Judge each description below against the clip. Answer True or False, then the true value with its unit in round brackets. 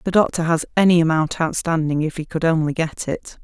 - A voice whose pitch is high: False (165 Hz)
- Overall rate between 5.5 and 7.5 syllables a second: True (5.6 syllables/s)